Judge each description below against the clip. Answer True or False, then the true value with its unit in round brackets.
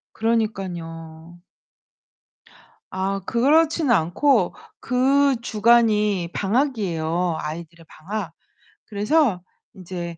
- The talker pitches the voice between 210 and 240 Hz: False (200 Hz)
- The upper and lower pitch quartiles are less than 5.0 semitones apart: False (5.6 semitones)